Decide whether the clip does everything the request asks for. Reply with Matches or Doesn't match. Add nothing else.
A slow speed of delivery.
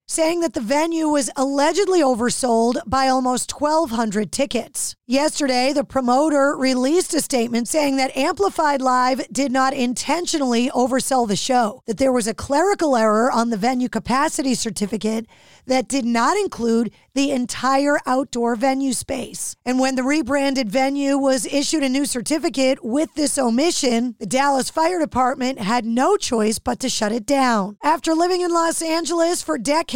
Doesn't match